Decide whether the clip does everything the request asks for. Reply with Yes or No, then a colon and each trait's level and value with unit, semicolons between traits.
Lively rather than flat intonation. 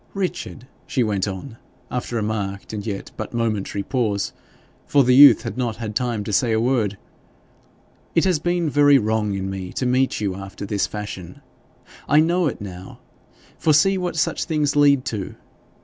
Yes: wide, 5.9 semitones